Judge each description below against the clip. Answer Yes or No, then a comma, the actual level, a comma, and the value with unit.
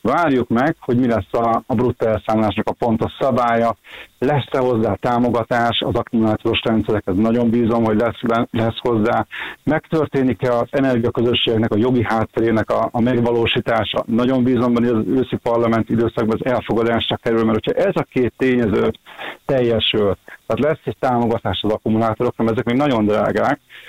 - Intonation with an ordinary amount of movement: No, narrow, 1.6 semitones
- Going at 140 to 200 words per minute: Yes, average, 150 wpm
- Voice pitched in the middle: No, low, 115 Hz